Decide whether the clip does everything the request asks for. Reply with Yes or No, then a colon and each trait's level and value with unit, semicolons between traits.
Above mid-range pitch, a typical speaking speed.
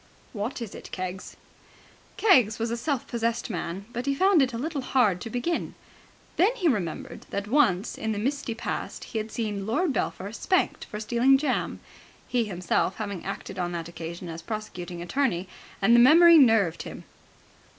Yes: high, 225 Hz; average, 175 wpm